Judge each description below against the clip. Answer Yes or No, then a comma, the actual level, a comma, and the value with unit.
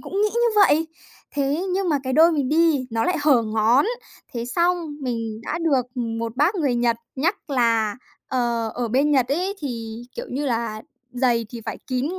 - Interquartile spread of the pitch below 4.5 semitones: No, average, 5.3 semitones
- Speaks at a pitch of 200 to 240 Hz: No, very high, 260 Hz